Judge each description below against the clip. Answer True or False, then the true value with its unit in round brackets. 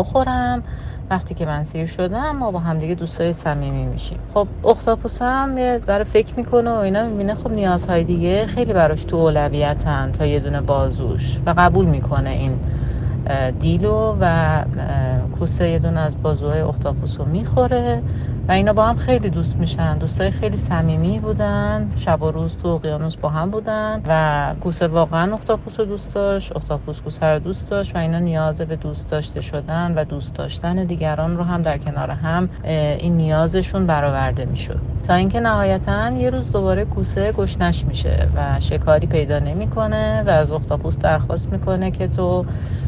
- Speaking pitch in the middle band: True (155 Hz)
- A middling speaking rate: False (160 wpm)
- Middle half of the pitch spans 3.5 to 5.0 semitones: False (5.5 semitones)